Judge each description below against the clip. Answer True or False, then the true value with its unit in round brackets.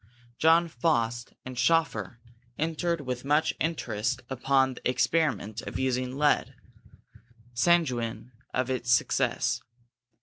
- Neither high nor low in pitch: False (130 Hz)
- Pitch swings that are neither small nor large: True (4.7 semitones)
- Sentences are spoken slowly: True (105 wpm)